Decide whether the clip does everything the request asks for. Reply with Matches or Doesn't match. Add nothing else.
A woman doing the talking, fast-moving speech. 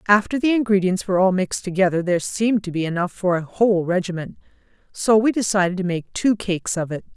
Matches